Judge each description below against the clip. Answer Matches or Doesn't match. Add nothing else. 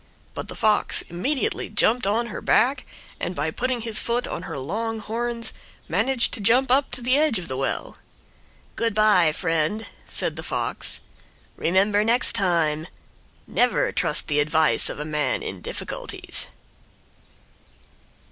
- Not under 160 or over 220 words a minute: Doesn't match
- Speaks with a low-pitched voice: Doesn't match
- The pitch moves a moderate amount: Doesn't match